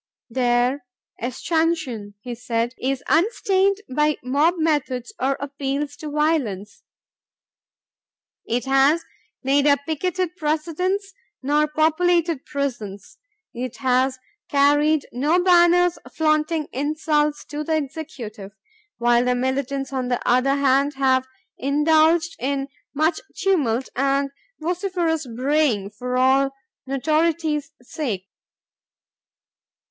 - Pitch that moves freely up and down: No, average, 3.6 semitones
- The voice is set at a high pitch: Yes, very high, 285 Hz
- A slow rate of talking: Yes, slow, 100 wpm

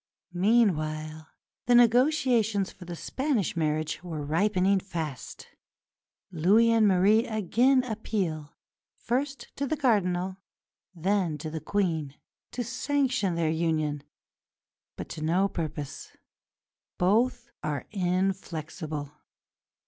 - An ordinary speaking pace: No, slow, 105 wpm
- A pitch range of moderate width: No, wide, 6.5 semitones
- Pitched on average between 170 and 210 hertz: Yes, medium, 185 Hz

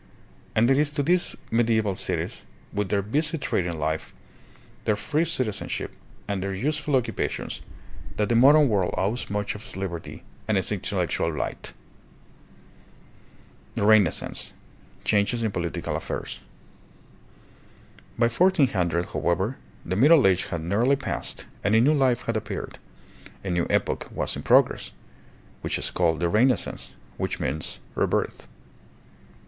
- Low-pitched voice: Yes, low, 105 Hz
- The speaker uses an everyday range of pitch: No, wide, 6.1 semitones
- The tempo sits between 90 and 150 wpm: Yes, average, 145 wpm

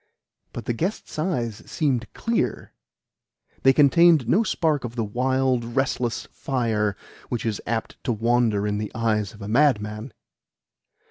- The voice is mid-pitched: No, low, 120 Hz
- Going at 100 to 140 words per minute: Yes, slow, 135 wpm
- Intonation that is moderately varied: Yes, average, 3.6 semitones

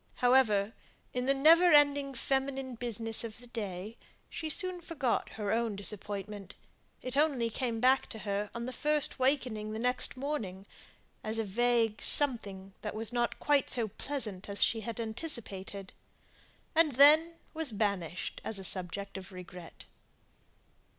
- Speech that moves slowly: No, average, 145 wpm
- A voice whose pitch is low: No, high, 230 Hz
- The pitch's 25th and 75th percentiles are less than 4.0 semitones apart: No, average, 4.9 semitones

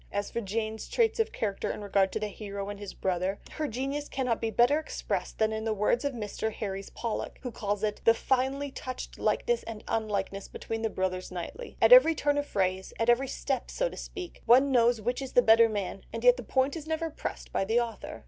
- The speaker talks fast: Yes, fast, 225 wpm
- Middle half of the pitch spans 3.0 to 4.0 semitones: No, average, 4.8 semitones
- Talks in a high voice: Yes, high, 230 Hz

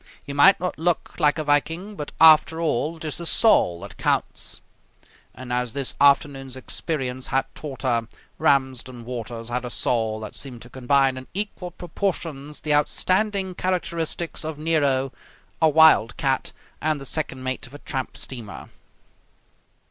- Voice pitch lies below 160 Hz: Yes, medium, 140 Hz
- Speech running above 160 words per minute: No, average, 155 wpm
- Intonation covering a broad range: No, average, 3.9 semitones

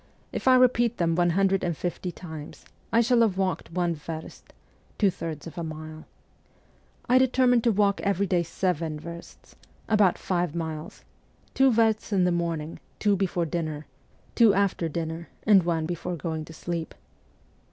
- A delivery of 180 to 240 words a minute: No, average, 165 wpm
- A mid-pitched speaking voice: Yes, medium, 175 Hz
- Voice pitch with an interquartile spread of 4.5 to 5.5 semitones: No, average, 3.7 semitones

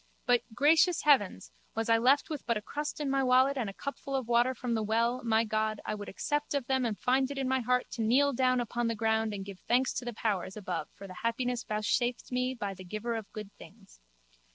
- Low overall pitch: No, high, 240 Hz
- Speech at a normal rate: No, fast, 240 wpm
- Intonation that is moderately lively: Yes, average, 3.2 semitones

